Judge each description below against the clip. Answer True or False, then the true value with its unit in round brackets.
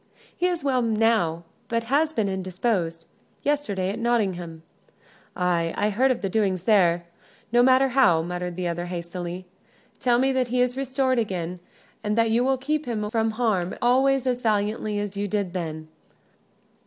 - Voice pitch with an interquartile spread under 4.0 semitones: False (5.6 semitones)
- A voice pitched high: True (215 Hz)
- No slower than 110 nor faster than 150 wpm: False (170 wpm)